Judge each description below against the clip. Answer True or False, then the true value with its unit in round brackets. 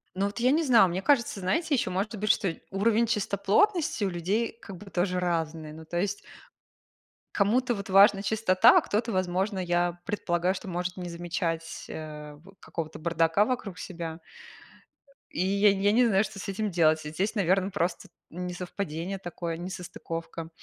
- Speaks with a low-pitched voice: False (185 Hz)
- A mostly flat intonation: False (3.2 semitones)